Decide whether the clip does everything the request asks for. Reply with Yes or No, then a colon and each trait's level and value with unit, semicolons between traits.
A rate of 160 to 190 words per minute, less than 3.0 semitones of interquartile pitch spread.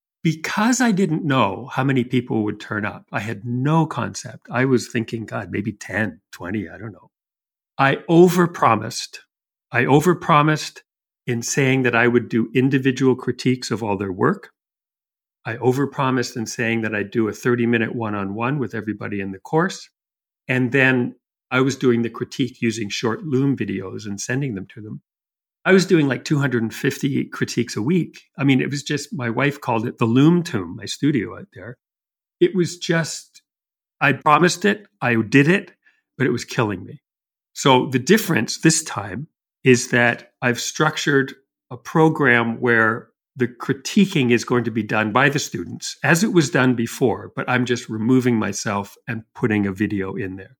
No: average, 180 wpm; average, 4.3 semitones